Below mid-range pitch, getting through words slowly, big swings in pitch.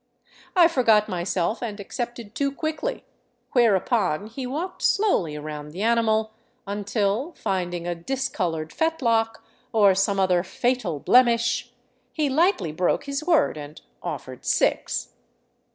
No: high, 220 Hz; slow, 120 wpm; wide, 6.5 semitones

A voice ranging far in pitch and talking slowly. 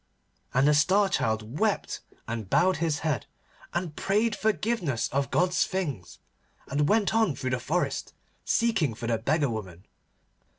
No: wide, 7.9 semitones; average, 145 wpm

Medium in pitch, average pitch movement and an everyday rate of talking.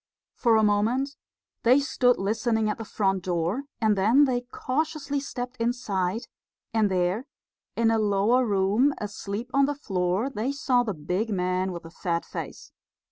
No: high, 220 Hz; average, 4.6 semitones; average, 160 wpm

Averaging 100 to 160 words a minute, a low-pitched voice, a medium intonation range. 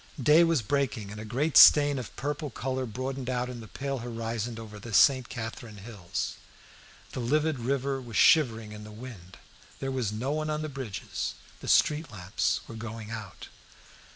No: average, 180 wpm; low, 120 Hz; average, 3.9 semitones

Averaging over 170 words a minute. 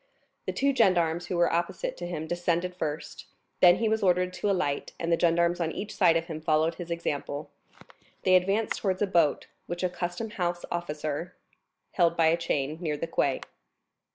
Yes: average, 185 wpm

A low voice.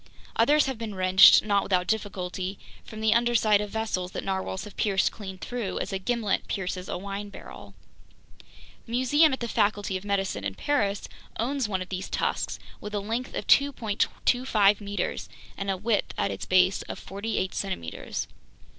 No: high, 205 Hz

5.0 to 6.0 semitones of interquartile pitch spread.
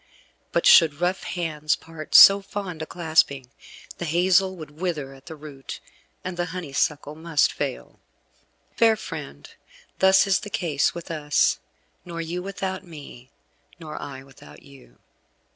No: average, 3.8 semitones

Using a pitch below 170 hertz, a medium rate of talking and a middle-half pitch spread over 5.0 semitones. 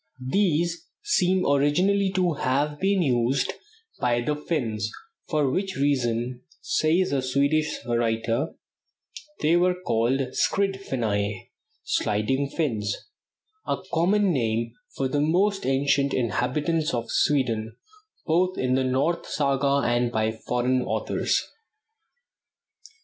No: medium, 140 Hz; slow, 110 wpm; wide, 5.6 semitones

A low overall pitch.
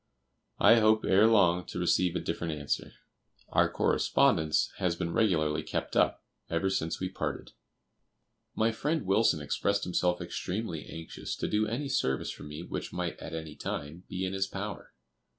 Yes: very low, 90 Hz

